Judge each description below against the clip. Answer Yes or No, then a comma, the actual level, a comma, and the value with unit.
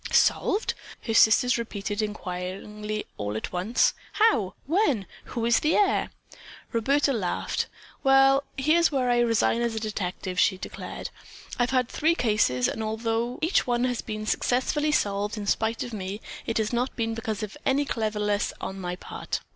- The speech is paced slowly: No, average, 165 wpm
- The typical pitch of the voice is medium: No, high, 225 Hz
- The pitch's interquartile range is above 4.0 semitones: No, average, 3.4 semitones